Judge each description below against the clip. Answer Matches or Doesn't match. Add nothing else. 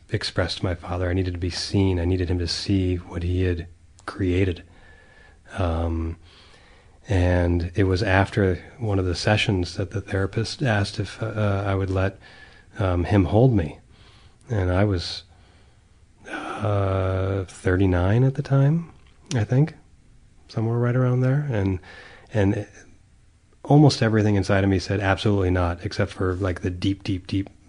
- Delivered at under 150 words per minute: Doesn't match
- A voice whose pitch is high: Doesn't match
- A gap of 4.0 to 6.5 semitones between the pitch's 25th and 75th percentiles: Doesn't match